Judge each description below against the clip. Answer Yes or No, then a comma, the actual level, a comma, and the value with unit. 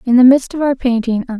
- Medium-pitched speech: No, very high, 250 Hz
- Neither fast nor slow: No, fast, 300 wpm